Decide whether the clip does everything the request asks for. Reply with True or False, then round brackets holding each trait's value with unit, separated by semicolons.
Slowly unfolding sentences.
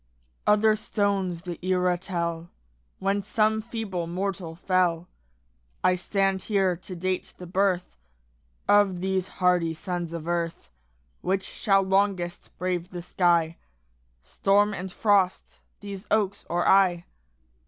True (120 wpm)